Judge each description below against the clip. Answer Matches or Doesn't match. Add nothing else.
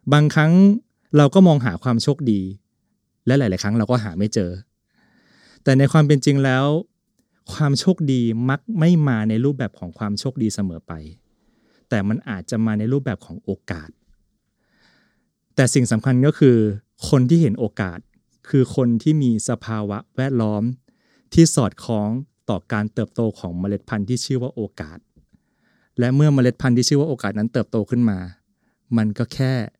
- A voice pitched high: Doesn't match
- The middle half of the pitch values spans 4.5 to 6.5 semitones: Matches